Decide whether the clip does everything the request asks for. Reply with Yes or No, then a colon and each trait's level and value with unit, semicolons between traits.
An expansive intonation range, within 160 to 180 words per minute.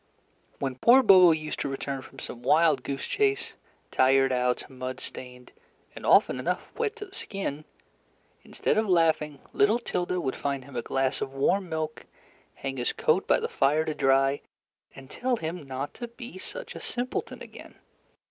Yes: wide, 6.6 semitones; average, 175 wpm